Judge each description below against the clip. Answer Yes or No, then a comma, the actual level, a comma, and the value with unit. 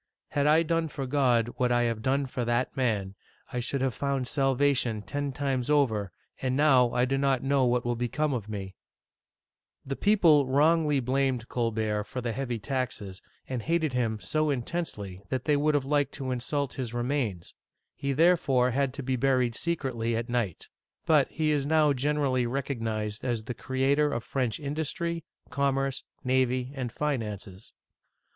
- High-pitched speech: No, low, 130 Hz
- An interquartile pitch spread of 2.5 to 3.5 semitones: Yes, average, 3.1 semitones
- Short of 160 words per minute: No, average, 165 wpm